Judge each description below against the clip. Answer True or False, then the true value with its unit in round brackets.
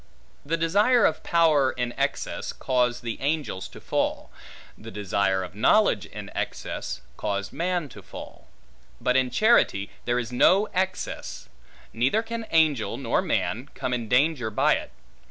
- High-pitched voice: False (130 Hz)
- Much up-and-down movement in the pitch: True (6.6 semitones)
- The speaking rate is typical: True (150 wpm)